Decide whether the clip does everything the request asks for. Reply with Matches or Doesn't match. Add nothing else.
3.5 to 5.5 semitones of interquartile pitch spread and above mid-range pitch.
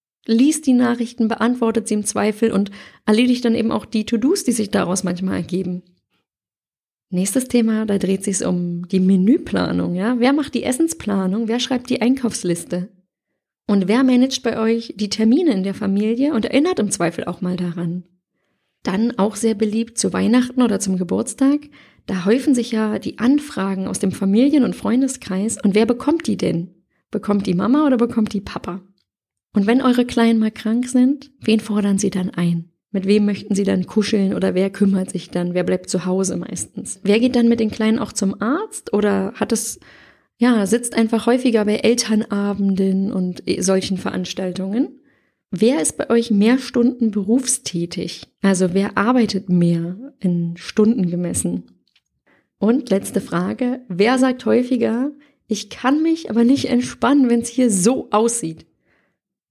Matches